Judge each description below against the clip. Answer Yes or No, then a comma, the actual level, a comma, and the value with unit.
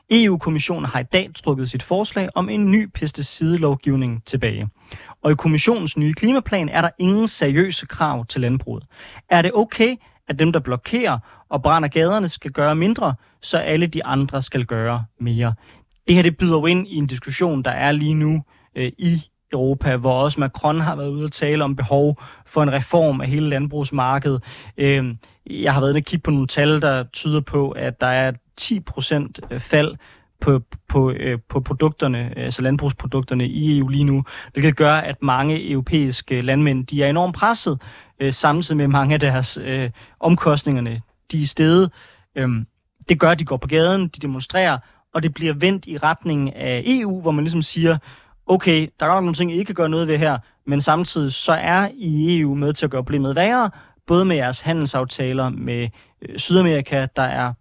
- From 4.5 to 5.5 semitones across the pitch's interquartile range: No, average, 4.0 semitones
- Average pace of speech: Yes, average, 185 wpm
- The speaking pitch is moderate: Yes, medium, 145 Hz